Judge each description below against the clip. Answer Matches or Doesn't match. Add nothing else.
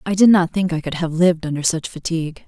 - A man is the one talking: Doesn't match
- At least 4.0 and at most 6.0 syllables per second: Doesn't match